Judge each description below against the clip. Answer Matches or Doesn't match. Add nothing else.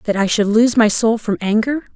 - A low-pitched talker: Doesn't match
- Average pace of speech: Doesn't match